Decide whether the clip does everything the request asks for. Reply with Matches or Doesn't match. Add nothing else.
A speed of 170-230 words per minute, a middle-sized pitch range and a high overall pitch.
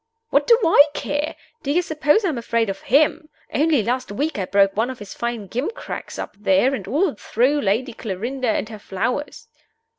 Doesn't match